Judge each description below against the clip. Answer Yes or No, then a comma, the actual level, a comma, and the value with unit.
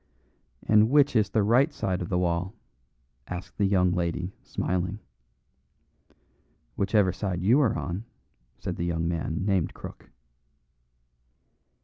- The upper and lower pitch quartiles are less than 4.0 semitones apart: Yes, average, 3.2 semitones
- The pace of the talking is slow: Yes, slow, 125 wpm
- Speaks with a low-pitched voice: Yes, very low, 95 Hz